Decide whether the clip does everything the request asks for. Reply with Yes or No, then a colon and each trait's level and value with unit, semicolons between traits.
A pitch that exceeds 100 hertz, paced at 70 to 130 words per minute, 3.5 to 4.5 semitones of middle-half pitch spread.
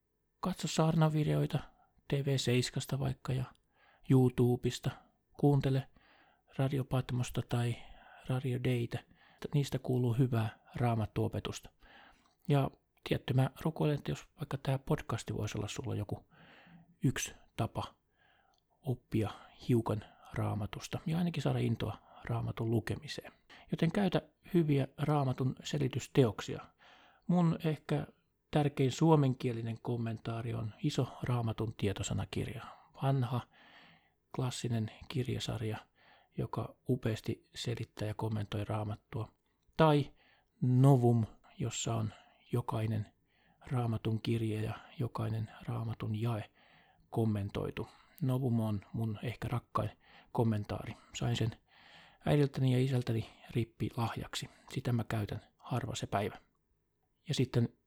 Yes: low, 120 Hz; average, 100 wpm; average, 3.8 semitones